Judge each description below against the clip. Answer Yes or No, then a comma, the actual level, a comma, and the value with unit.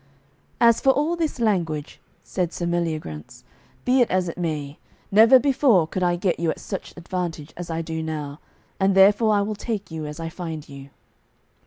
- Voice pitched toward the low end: No, medium, 175 Hz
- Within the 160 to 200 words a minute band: Yes, average, 185 wpm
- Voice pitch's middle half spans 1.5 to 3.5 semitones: No, average, 4.8 semitones